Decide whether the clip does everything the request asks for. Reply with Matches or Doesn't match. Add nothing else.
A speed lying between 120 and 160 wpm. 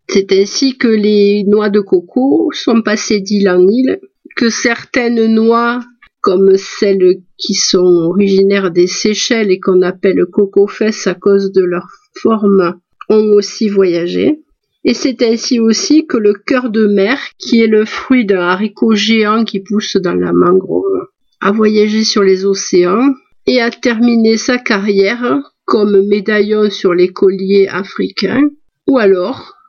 Matches